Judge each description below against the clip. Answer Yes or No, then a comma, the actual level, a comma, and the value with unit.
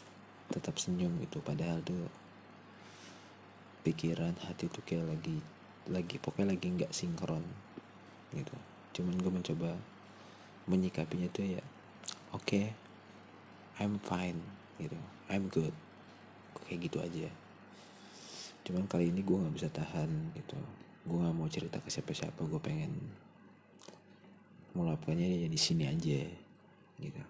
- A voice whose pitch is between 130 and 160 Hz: No, low, 105 Hz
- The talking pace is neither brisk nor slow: Yes, average, 120 wpm